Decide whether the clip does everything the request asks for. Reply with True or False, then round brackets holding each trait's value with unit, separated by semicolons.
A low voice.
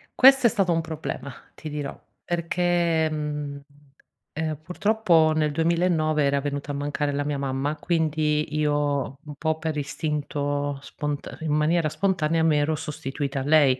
False (150 Hz)